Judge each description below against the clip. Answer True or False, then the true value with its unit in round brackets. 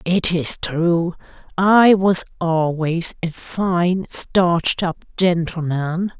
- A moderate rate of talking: False (105 wpm)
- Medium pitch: True (175 Hz)